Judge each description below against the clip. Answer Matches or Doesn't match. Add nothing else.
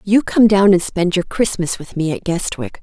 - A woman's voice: Matches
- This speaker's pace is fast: Matches